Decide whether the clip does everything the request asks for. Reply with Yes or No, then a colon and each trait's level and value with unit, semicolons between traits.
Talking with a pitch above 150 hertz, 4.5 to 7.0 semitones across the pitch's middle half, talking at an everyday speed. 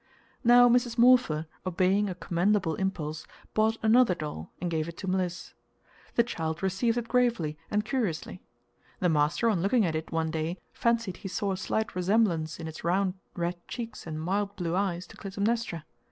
Yes: high, 190 Hz; average, 4.9 semitones; average, 175 wpm